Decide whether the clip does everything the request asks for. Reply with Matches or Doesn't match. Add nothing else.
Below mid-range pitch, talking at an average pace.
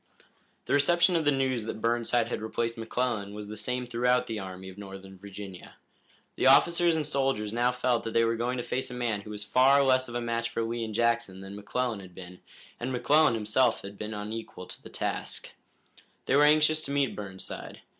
Doesn't match